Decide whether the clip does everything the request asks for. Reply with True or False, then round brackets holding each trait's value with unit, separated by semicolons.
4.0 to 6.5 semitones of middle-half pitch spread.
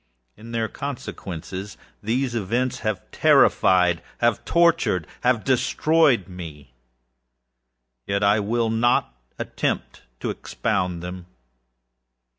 True (4.8 semitones)